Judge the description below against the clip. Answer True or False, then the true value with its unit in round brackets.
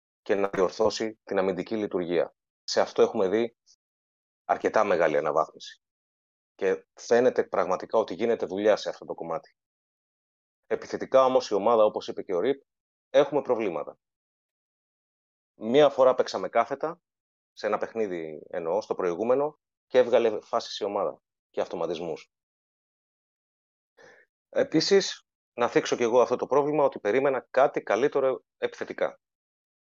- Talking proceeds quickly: False (130 wpm)